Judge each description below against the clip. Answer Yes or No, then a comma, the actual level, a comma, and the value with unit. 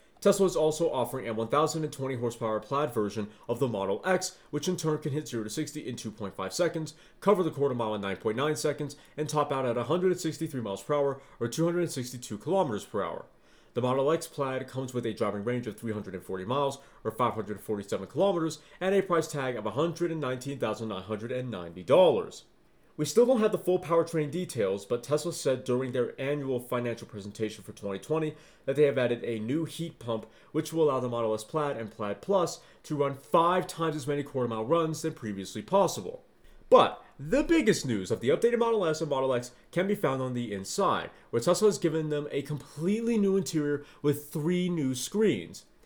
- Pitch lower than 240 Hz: Yes, medium, 140 Hz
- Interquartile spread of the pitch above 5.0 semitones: Yes, wide, 5.5 semitones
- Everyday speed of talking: Yes, average, 190 wpm